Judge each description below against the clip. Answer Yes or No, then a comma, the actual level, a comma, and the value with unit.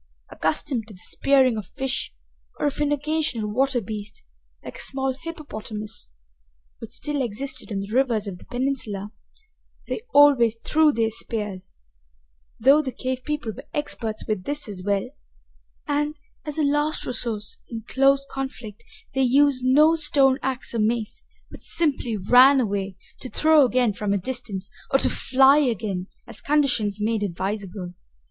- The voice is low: No, very high, 250 Hz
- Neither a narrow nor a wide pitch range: Yes, average, 4.9 semitones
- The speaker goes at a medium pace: Yes, average, 155 wpm